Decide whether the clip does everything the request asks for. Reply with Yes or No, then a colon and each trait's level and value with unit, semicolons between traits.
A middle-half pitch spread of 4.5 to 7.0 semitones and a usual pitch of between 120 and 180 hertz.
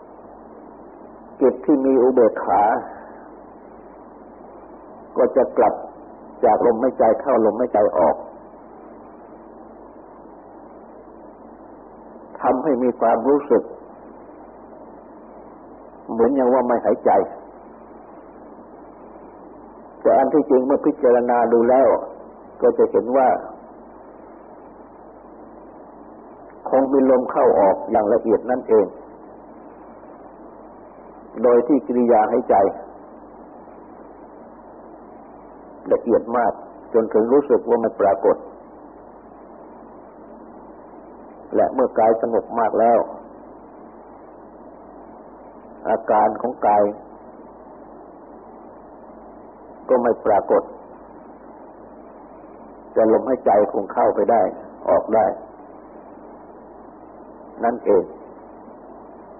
No: average, 2.7 semitones; low, 125 Hz